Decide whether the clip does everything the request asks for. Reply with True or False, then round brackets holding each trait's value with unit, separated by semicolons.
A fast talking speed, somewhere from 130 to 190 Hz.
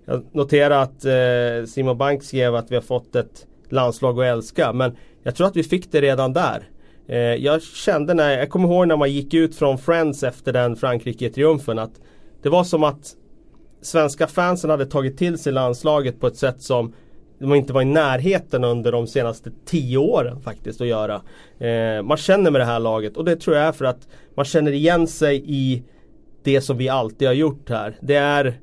True (205 wpm; 135 Hz)